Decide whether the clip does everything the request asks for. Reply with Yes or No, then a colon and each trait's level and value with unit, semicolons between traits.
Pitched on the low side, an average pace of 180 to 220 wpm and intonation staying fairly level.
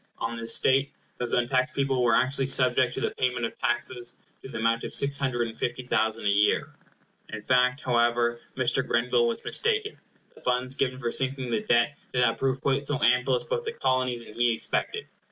Yes: low, 125 Hz; fast, 205 wpm; narrow, 1.9 semitones